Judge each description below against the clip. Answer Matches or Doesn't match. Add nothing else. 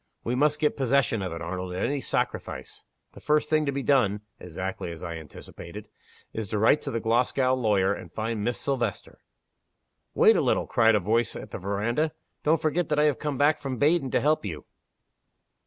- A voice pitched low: Matches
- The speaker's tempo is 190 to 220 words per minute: Matches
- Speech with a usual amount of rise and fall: Doesn't match